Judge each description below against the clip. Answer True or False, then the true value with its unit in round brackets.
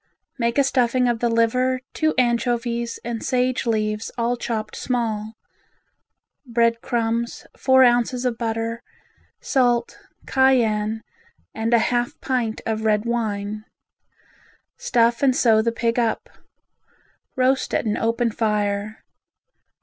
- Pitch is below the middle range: False (235 Hz)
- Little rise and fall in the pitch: True (1.8 semitones)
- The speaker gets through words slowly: True (120 wpm)